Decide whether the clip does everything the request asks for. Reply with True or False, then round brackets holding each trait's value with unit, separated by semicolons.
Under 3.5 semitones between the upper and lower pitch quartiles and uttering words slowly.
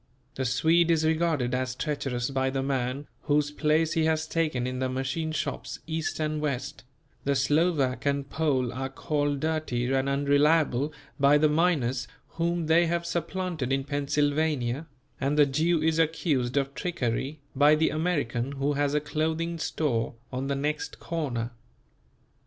False (3.1 semitones; 155 wpm)